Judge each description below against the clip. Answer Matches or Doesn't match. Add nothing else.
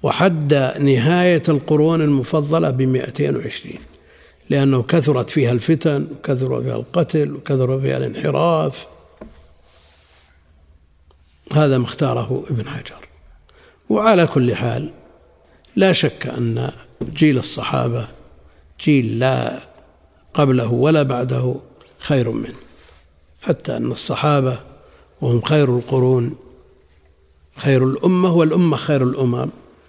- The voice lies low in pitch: Matches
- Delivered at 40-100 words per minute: Matches